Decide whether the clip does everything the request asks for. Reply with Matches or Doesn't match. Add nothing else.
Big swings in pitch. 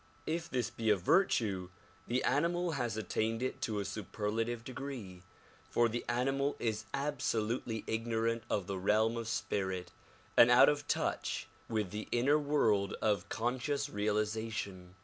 Doesn't match